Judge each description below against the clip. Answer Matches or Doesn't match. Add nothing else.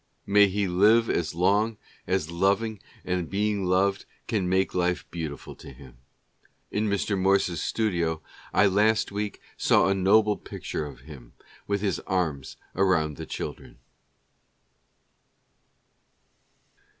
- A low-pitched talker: Matches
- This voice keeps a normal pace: Doesn't match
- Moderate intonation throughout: Matches